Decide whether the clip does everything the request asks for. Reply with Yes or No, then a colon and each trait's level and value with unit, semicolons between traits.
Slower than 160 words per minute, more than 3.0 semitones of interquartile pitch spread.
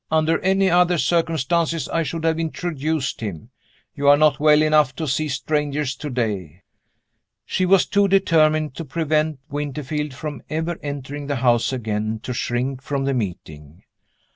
Yes: average, 150 wpm; average, 3.7 semitones